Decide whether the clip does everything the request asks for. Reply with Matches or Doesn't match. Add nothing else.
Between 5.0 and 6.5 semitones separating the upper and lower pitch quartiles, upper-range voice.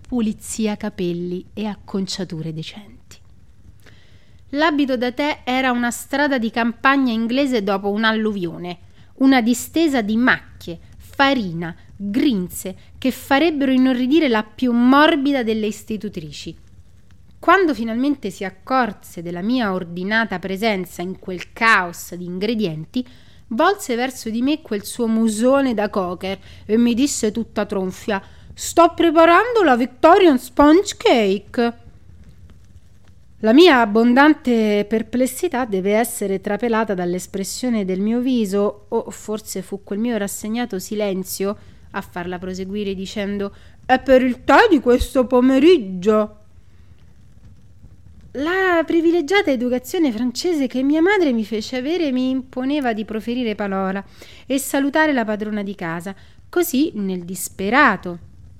Matches